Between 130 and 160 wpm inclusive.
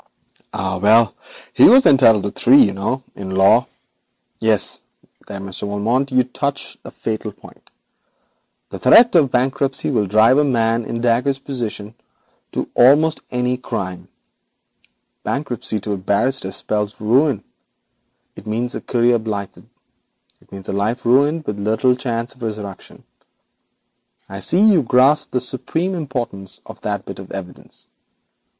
Yes: average, 145 wpm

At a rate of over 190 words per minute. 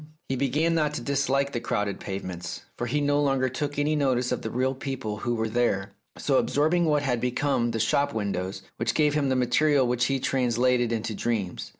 Yes: average, 200 wpm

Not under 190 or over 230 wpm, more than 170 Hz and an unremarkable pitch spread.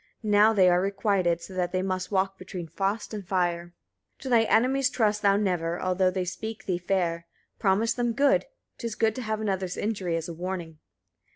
Yes: average, 195 wpm; high, 190 Hz; average, 3.4 semitones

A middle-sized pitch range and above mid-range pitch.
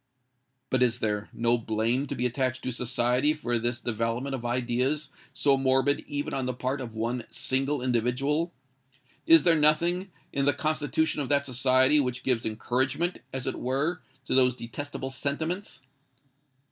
No: average, 3.0 semitones; low, 130 Hz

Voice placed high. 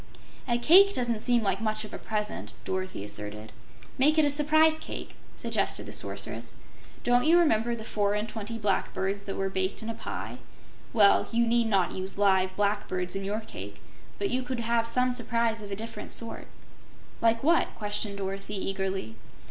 Yes: high, 215 Hz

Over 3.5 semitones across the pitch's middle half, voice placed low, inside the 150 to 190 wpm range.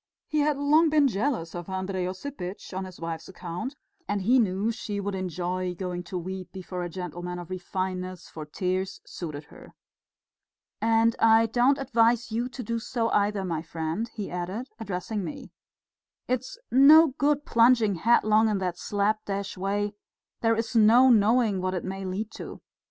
No: average, 4.1 semitones; high, 200 Hz; average, 165 wpm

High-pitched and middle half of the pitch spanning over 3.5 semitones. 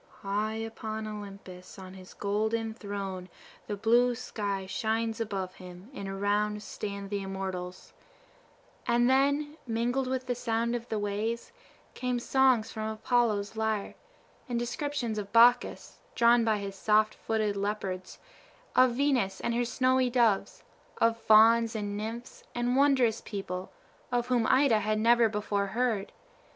No: high, 220 Hz; average, 3.0 semitones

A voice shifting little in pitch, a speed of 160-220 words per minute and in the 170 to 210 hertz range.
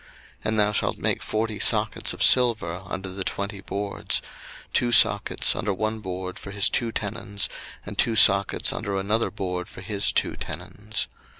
No: narrow, 2.0 semitones; average, 170 wpm; low, 100 Hz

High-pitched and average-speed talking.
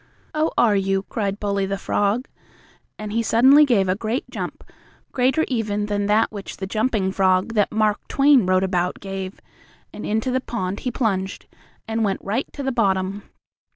Yes: high, 210 Hz; average, 175 wpm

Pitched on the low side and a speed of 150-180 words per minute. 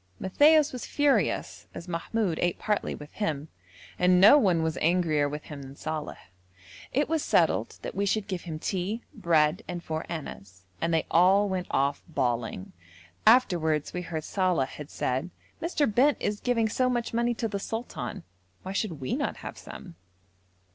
No: medium, 180 Hz; average, 170 wpm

